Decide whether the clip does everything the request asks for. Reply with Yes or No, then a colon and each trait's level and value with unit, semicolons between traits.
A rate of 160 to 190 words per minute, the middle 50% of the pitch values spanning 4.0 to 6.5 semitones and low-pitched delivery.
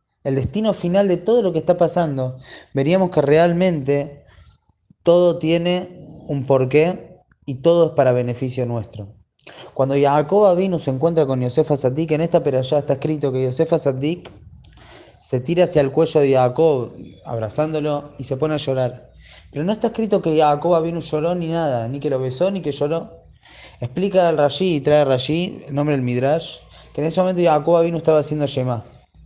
No: average, 185 wpm; average, 4.3 semitones; medium, 150 Hz